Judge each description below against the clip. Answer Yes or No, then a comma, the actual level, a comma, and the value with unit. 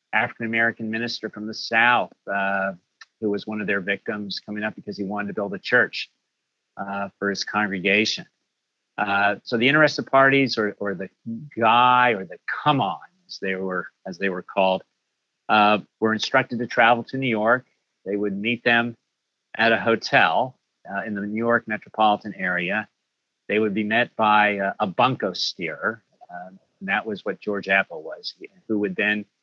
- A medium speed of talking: Yes, average, 175 wpm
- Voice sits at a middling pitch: No, low, 105 Hz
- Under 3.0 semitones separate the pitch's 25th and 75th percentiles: Yes, narrow, 2.5 semitones